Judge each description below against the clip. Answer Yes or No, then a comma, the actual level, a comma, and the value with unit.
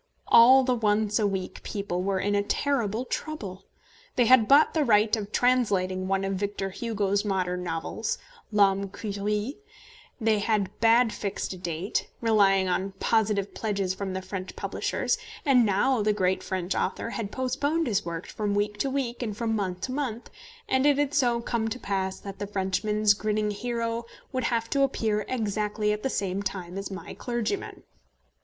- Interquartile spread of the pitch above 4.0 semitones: No, average, 3.2 semitones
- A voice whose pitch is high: Yes, high, 210 Hz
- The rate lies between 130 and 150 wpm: No, average, 175 wpm